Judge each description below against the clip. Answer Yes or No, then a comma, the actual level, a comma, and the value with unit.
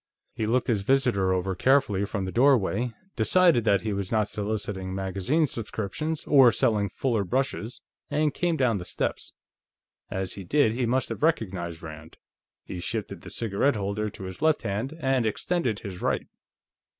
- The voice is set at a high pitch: No, low, 110 Hz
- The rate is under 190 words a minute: Yes, average, 165 wpm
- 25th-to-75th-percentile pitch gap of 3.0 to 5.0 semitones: No, wide, 5.4 semitones